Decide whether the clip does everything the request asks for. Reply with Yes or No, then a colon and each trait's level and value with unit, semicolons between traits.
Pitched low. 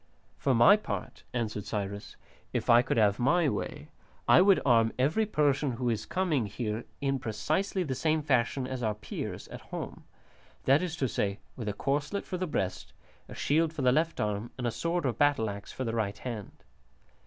Yes: low, 130 Hz